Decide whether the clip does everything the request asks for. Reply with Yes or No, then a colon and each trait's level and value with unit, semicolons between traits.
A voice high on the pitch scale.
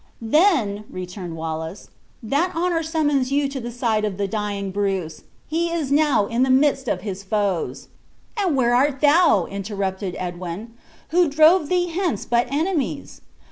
Yes: high, 240 Hz